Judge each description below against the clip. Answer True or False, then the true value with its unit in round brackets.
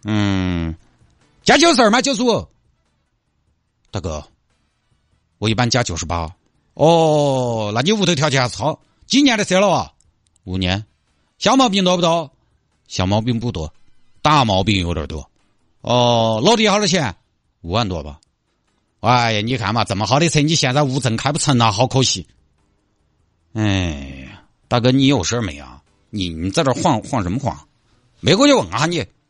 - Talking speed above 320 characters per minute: False (230 characters per minute)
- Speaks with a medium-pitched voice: False (110 Hz)